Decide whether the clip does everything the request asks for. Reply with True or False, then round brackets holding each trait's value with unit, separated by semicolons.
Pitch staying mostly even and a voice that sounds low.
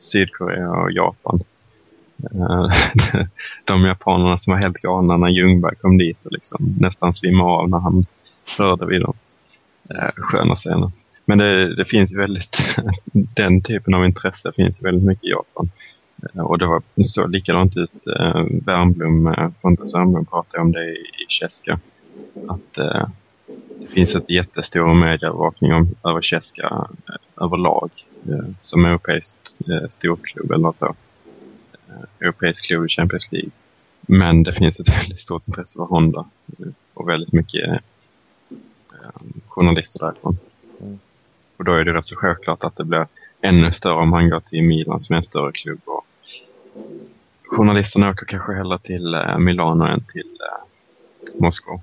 True (1.9 semitones; 90 Hz)